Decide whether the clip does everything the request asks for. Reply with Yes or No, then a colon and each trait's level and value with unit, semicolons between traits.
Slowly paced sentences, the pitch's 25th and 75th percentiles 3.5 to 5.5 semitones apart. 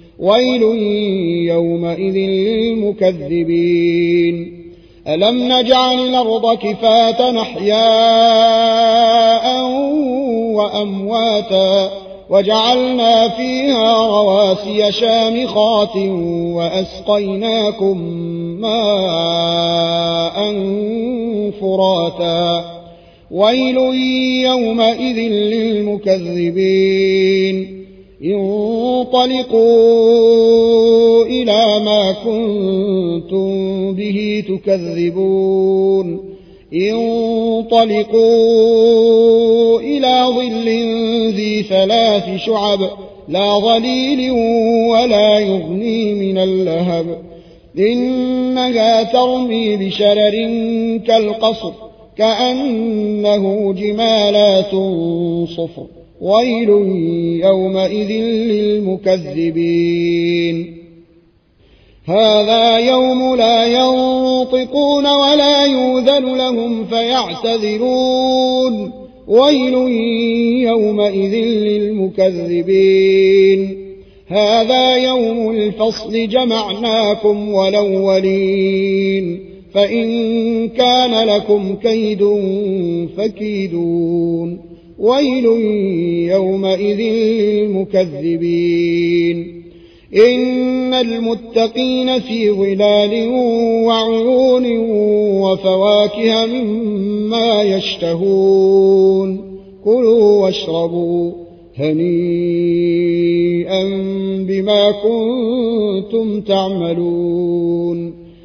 No: slow, 45 wpm; average, 3.1 semitones